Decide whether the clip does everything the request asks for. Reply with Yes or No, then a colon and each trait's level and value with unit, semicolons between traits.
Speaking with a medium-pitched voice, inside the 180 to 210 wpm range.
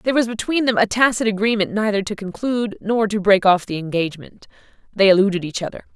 No: high, 210 Hz; average, 200 wpm